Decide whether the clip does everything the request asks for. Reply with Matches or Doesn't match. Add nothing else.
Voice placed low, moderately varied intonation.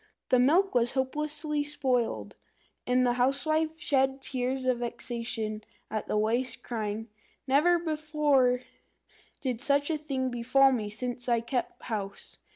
Doesn't match